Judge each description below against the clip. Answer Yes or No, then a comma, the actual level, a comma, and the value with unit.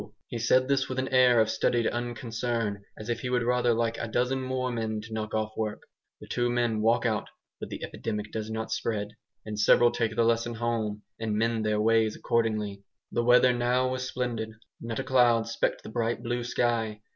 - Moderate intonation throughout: No, narrow, 1.8 semitones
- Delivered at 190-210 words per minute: Yes, fast, 205 wpm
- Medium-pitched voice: No, low, 115 Hz